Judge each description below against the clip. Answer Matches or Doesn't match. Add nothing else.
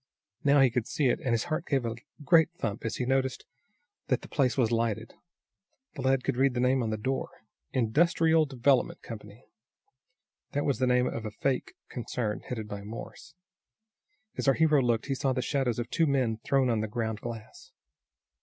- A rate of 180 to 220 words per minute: Matches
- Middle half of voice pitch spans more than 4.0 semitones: Doesn't match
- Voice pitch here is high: Doesn't match